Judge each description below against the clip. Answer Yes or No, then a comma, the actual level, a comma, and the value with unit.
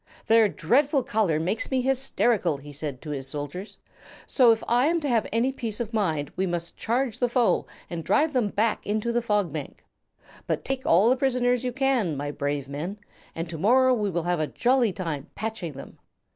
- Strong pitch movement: Yes, wide, 7.1 semitones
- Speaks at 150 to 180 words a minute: No, average, 200 wpm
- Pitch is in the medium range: No, high, 215 Hz